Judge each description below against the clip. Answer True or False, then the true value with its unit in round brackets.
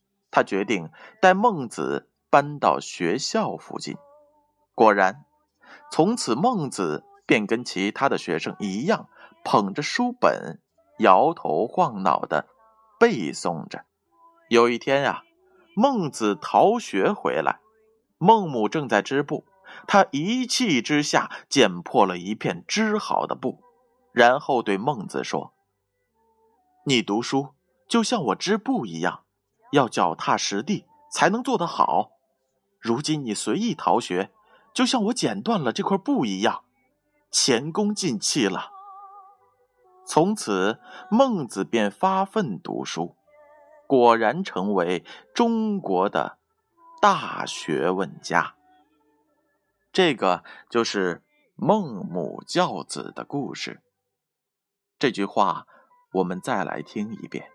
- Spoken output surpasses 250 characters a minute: False (165 characters per minute)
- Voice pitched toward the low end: False (200 Hz)